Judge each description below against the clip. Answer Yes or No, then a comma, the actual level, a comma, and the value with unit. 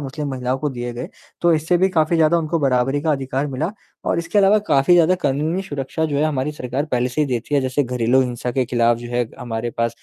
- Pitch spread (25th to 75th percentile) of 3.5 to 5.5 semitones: Yes, average, 3.9 semitones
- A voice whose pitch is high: No, low, 135 Hz